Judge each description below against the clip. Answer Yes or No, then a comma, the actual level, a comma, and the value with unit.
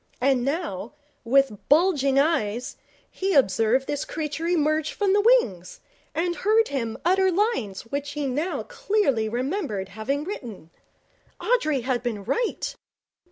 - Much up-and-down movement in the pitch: Yes, wide, 7.2 semitones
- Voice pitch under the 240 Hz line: No, very high, 280 Hz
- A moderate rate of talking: No, slow, 130 wpm